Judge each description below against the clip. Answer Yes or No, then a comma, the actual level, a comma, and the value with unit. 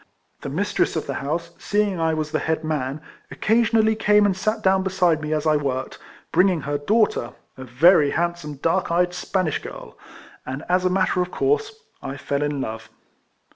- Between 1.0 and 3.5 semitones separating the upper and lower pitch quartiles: No, average, 4.6 semitones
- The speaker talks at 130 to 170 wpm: No, average, 185 wpm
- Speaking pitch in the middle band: Yes, medium, 170 Hz